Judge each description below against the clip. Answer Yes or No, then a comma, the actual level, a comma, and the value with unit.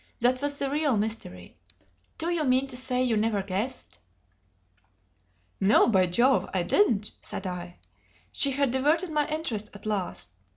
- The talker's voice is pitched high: Yes, high, 245 Hz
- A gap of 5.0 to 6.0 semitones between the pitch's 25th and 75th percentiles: Yes, wide, 5.6 semitones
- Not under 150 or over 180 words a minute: Yes, average, 155 wpm